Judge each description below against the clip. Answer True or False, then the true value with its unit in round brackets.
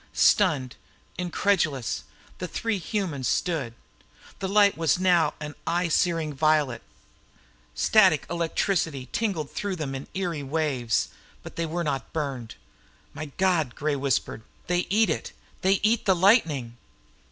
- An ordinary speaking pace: False (130 wpm)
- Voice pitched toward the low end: False (160 Hz)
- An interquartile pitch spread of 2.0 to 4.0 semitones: False (4.9 semitones)